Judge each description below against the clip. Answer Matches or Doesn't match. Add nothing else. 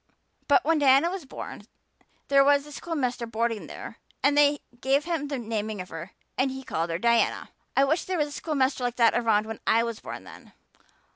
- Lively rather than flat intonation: Doesn't match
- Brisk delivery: Matches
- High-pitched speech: Matches